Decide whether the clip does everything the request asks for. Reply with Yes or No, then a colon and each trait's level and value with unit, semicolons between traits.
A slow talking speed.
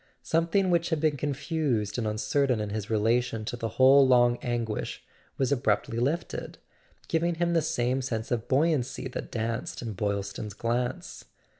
No: average, 155 wpm